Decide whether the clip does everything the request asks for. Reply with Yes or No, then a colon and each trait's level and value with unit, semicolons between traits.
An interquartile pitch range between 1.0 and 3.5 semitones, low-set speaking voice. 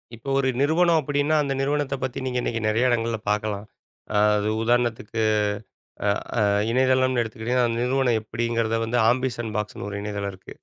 Yes: average, 2.8 semitones; low, 120 Hz